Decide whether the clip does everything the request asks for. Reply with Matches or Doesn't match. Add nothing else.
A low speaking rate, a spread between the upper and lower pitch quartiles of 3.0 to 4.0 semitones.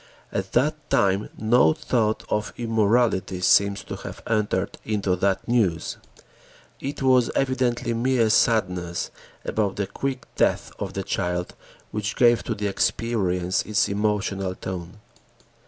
Matches